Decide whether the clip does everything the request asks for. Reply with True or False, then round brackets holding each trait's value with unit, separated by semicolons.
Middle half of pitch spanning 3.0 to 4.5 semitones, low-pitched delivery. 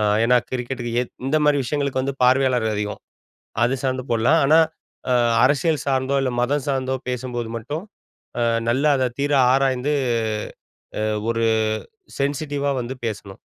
False (2.5 semitones; 130 Hz)